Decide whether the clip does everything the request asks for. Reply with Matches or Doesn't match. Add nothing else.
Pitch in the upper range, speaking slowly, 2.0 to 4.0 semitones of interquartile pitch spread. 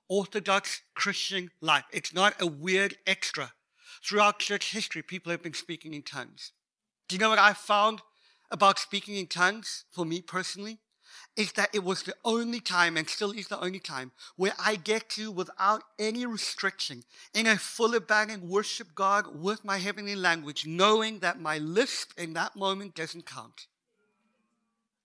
Doesn't match